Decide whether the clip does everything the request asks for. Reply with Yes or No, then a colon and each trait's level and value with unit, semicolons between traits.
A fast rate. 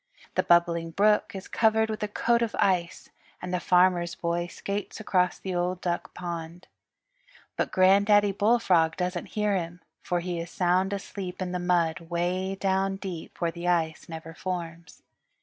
No: average, 165 wpm